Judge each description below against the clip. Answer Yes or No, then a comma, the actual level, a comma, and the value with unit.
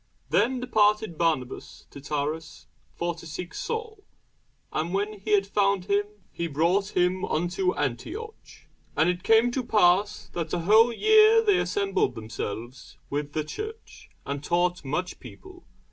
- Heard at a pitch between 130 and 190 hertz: Yes, medium, 185 Hz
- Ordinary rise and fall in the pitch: No, wide, 6.5 semitones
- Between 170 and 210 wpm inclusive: No, average, 145 wpm